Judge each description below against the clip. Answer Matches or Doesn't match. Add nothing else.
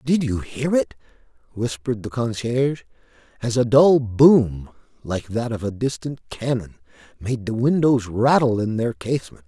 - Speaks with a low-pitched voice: Matches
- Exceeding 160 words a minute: Doesn't match